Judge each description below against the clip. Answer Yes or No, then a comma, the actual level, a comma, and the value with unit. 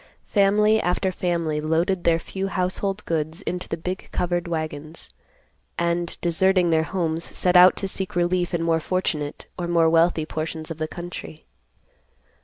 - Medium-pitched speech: Yes, medium, 170 Hz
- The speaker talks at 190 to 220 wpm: No, average, 155 wpm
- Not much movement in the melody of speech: Yes, narrow, 2.1 semitones